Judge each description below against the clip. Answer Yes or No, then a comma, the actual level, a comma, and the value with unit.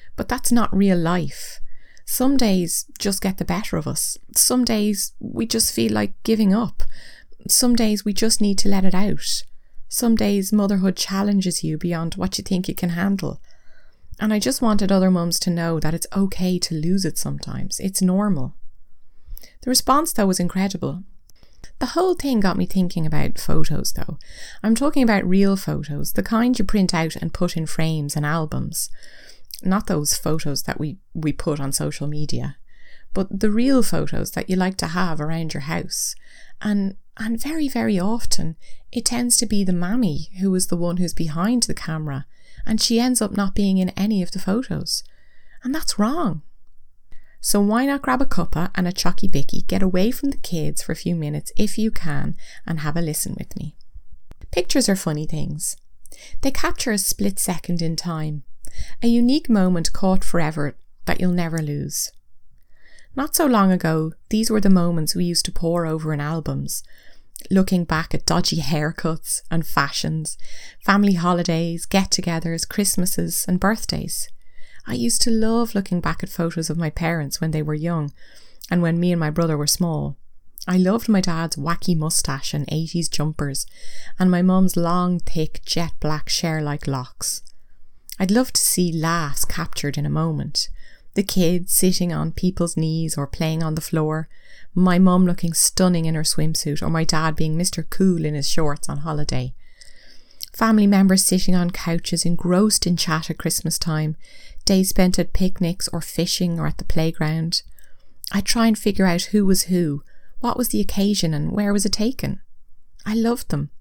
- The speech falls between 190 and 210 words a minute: No, average, 180 wpm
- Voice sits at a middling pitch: Yes, medium, 180 Hz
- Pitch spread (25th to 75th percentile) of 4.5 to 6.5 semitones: No, average, 4.1 semitones